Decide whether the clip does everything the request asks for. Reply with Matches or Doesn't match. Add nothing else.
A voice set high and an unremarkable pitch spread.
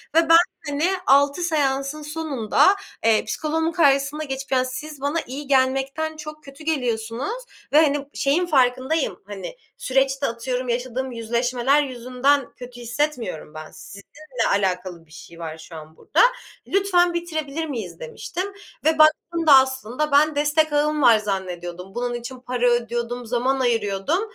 Matches